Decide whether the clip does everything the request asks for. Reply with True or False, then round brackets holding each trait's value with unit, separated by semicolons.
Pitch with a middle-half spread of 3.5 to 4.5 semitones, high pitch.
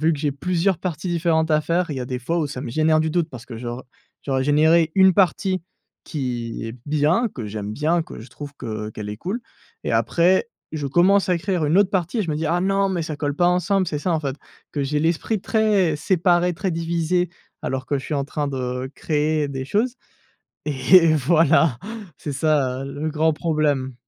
False (4.1 semitones; 155 Hz)